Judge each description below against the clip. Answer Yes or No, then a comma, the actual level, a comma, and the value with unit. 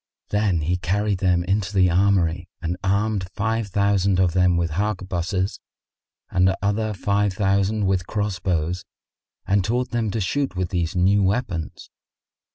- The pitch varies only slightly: Yes, narrow, 2.3 semitones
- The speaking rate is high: No, average, 150 wpm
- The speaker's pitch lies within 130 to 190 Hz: No, very low, 95 Hz